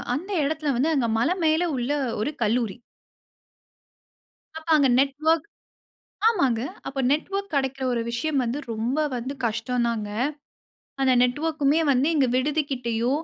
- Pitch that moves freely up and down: No, average, 4.3 semitones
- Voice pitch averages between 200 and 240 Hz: No, very high, 270 Hz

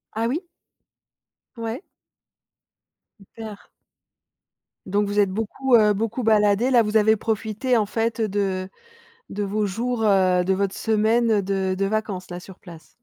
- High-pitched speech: Yes, high, 210 Hz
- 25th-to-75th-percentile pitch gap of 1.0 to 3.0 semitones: Yes, narrow, 2.4 semitones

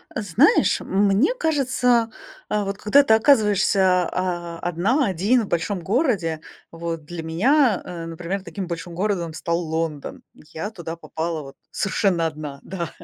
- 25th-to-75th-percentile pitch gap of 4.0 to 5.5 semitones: Yes, average, 4.4 semitones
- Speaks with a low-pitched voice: No, medium, 185 Hz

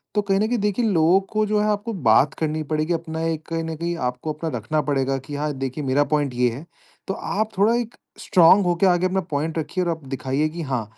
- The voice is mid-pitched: Yes, medium, 160 Hz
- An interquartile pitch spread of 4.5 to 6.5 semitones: Yes, average, 4.9 semitones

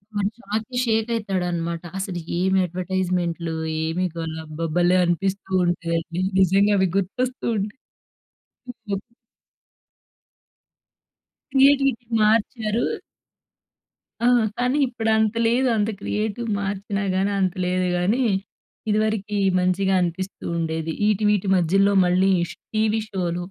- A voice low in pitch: No, high, 195 Hz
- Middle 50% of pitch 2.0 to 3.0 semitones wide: No, average, 3.4 semitones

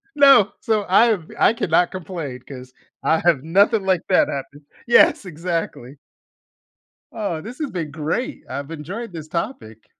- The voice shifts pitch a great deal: Yes, wide, 5.7 semitones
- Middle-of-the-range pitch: Yes, medium, 170 Hz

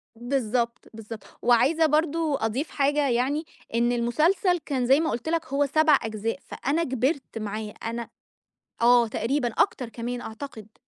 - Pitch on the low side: No, very high, 250 Hz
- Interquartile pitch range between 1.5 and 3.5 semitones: No, average, 4.2 semitones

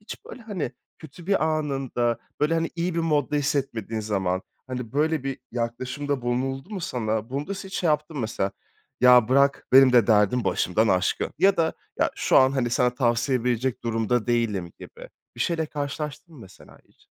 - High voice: No, low, 130 Hz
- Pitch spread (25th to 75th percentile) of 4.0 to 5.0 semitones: Yes, average, 4.4 semitones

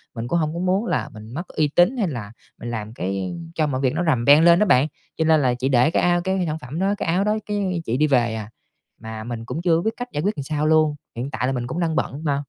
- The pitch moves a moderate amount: No, wide, 6.1 semitones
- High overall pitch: No, medium, 150 Hz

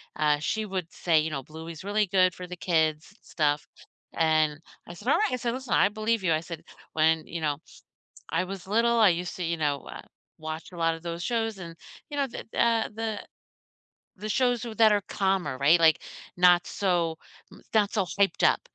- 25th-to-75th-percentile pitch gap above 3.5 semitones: Yes, average, 5.0 semitones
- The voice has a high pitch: No, medium, 180 Hz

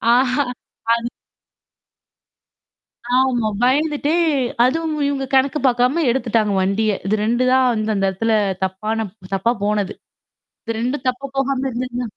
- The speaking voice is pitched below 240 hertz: No, high, 245 Hz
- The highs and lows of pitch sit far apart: No, average, 3.5 semitones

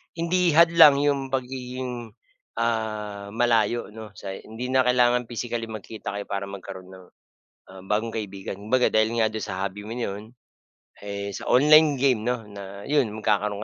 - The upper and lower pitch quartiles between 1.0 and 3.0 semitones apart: No, average, 3.6 semitones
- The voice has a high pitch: No, low, 110 Hz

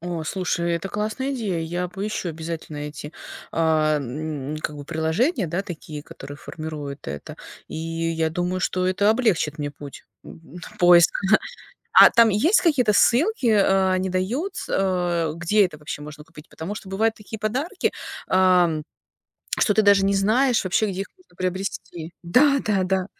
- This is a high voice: No, medium, 180 Hz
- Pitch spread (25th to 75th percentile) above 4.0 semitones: Yes, average, 4.7 semitones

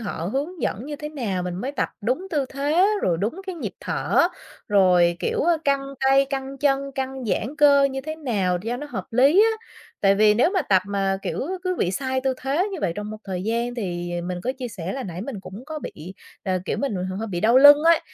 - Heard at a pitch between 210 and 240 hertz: No, very high, 255 Hz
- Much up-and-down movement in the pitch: Yes, wide, 6.4 semitones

